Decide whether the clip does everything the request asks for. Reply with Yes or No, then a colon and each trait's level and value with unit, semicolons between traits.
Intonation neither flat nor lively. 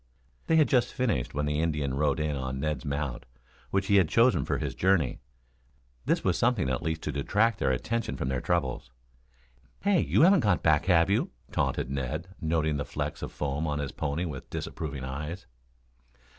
No: wide, 5.7 semitones